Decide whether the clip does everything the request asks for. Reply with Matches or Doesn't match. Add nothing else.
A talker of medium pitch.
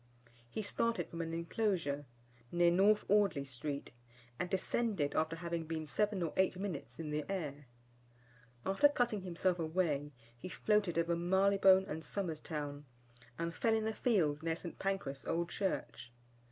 Matches